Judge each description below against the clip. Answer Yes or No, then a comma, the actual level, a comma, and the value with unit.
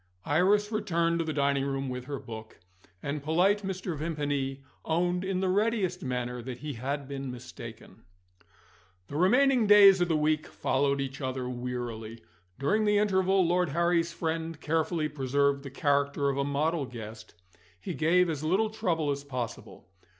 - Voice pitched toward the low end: No, medium, 150 Hz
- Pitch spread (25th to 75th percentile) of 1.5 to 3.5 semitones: No, average, 4.8 semitones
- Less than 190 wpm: Yes, average, 160 wpm